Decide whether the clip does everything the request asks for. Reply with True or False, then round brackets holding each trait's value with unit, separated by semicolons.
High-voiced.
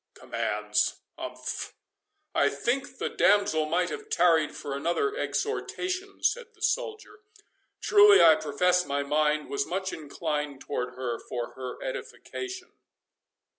False (175 Hz)